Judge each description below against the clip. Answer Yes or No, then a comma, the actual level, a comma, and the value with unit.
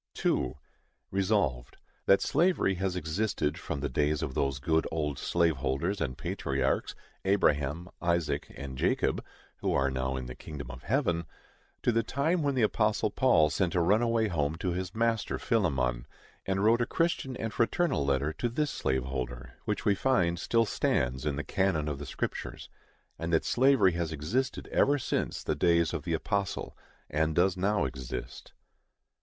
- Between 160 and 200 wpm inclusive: Yes, average, 170 wpm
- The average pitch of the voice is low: Yes, very low, 85 Hz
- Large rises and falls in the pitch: Yes, wide, 7.3 semitones